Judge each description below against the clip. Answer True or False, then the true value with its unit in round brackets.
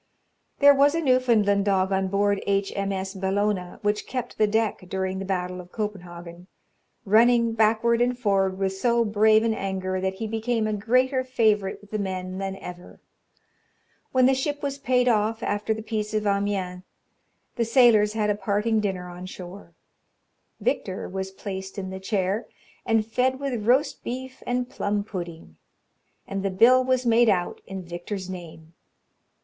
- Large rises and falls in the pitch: False (3.5 semitones)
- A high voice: True (205 Hz)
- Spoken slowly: False (165 wpm)